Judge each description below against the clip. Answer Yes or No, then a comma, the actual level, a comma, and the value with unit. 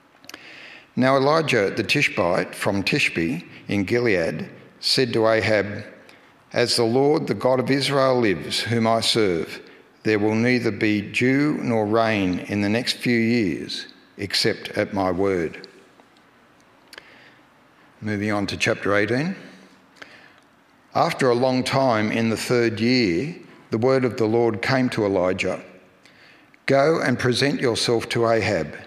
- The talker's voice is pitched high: No, low, 115 Hz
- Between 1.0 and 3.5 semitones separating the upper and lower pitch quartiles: Yes, average, 3.1 semitones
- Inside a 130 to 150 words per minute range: Yes, slow, 135 wpm